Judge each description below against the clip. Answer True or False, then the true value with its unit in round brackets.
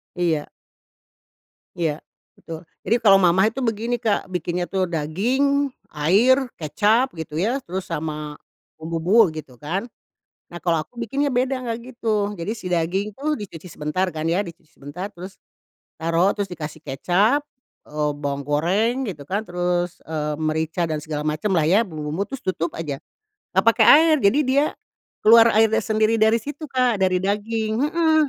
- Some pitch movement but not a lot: False (6.1 semitones)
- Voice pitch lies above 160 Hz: True (185 Hz)